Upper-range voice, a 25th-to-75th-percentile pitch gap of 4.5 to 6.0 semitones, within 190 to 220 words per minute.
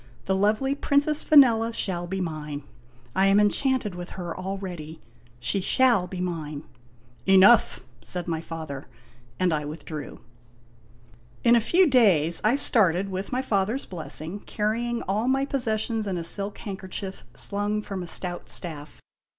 No: high, 195 Hz; average, 5.0 semitones; average, 155 wpm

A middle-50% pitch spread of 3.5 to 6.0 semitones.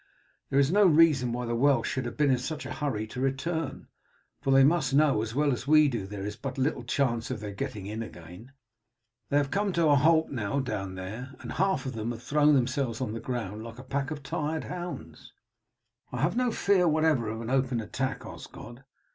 Yes: average, 4.4 semitones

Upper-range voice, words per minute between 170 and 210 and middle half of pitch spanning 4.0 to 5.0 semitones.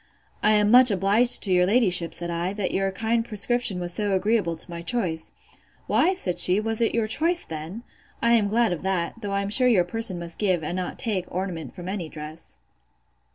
Yes: high, 195 Hz; fast, 205 wpm; average, 4.3 semitones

